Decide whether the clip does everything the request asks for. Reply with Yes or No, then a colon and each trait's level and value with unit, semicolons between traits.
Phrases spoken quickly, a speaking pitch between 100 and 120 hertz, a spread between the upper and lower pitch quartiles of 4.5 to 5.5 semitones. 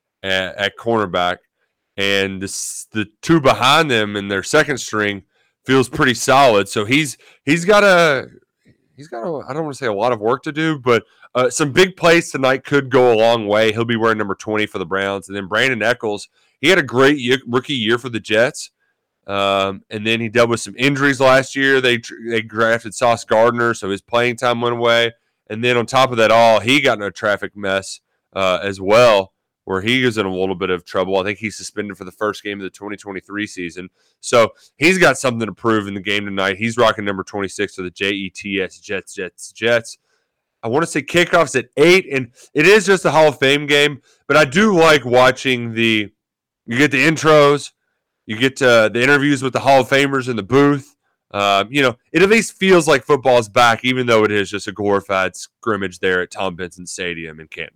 Yes: fast, 215 wpm; low, 115 Hz; average, 5.1 semitones